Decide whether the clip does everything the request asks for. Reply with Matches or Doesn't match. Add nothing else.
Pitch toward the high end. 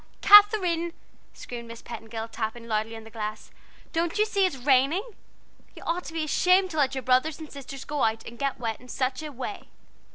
Matches